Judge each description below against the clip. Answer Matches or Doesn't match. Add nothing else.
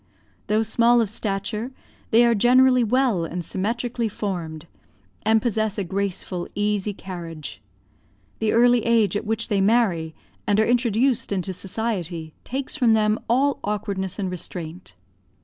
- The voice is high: Matches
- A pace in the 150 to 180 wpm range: Doesn't match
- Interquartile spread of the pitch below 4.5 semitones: Matches